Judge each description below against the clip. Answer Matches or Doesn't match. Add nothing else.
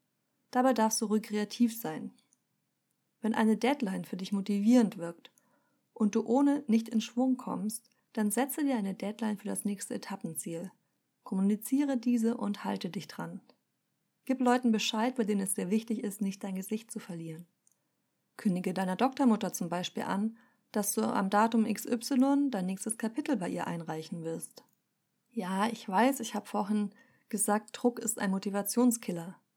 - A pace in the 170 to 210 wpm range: Doesn't match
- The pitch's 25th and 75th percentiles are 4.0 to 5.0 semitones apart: Doesn't match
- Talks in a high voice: Matches